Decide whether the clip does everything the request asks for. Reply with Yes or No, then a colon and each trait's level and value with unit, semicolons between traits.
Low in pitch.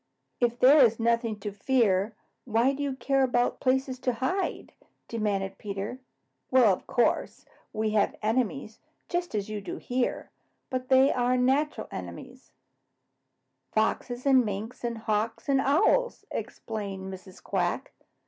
No: high, 235 Hz